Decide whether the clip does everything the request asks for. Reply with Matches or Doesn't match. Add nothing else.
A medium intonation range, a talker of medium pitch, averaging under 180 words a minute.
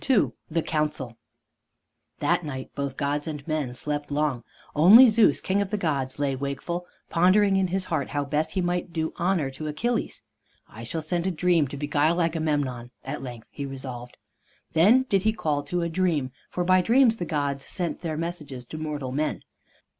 Doesn't match